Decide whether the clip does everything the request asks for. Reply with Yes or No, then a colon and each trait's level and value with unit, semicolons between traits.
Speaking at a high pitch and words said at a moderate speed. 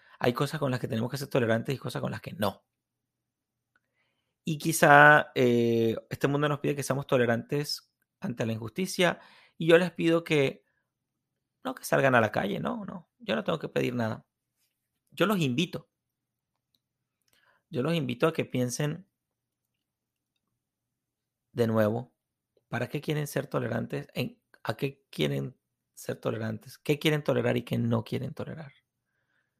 No: low, 135 Hz; average, 155 wpm